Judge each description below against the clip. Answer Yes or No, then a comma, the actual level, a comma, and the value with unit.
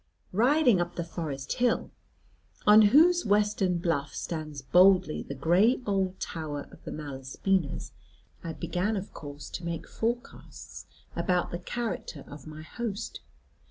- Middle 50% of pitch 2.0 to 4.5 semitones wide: No, average, 5.3 semitones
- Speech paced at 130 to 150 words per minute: Yes, slow, 135 wpm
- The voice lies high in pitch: No, medium, 175 Hz